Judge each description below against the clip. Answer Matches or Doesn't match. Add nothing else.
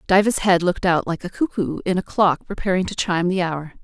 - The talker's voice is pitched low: Doesn't match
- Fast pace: Matches